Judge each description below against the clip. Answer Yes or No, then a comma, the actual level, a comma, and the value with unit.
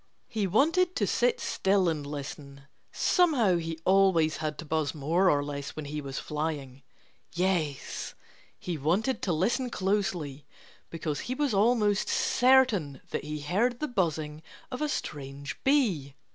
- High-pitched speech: No, medium, 170 Hz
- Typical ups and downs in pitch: No, wide, 6.8 semitones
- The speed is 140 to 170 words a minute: Yes, average, 145 wpm